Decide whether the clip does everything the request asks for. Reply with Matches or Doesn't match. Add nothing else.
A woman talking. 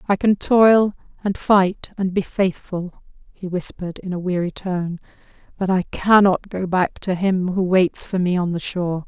Matches